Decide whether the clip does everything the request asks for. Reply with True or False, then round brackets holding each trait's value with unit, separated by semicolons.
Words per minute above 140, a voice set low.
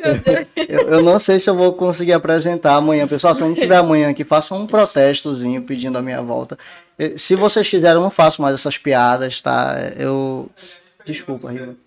False (180 wpm; 155 Hz)